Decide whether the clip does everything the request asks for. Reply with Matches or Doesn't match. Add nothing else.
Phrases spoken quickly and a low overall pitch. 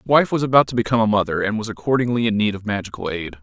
Matches